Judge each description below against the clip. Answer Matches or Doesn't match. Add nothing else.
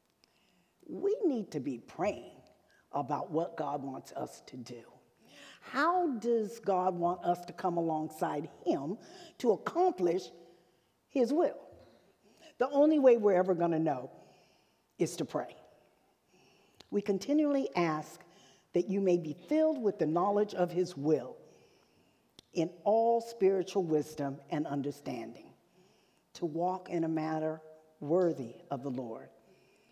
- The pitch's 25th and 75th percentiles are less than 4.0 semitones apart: Doesn't match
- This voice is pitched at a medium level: Matches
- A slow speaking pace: Matches